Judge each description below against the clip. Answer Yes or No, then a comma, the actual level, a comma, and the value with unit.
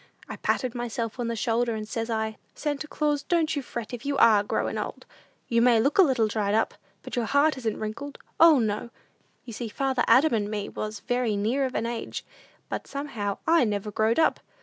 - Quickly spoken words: Yes, fast, 210 wpm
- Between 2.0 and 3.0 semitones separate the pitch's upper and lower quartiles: No, average, 4.1 semitones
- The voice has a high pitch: Yes, high, 235 Hz